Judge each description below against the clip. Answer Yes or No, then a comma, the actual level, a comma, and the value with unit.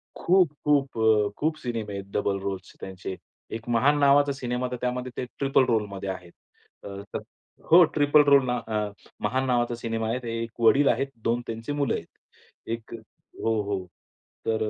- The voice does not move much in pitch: No, average, 3.9 semitones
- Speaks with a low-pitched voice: Yes, low, 120 Hz